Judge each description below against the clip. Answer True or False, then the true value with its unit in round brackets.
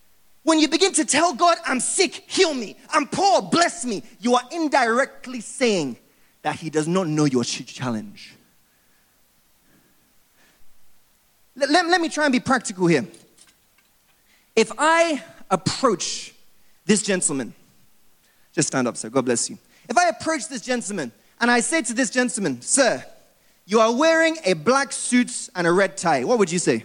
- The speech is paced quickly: False (160 wpm)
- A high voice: True (245 Hz)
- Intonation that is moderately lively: False (8.9 semitones)